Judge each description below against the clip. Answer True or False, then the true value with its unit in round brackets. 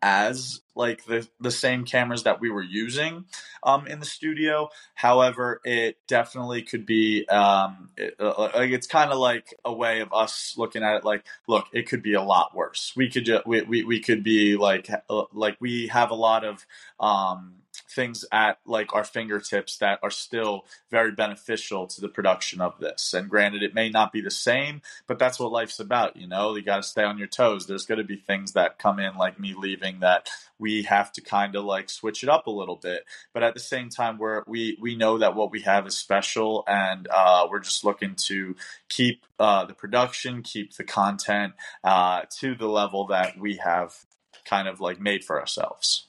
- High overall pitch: False (110 Hz)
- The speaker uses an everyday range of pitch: True (3.0 semitones)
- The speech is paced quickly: True (210 wpm)